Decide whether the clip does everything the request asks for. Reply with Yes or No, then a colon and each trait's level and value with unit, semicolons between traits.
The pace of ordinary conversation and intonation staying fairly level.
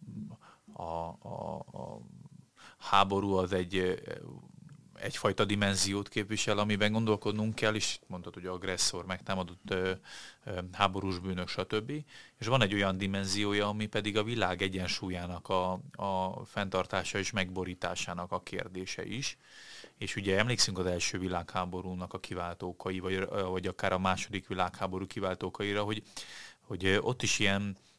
Yes: average, 125 wpm; narrow, 2.1 semitones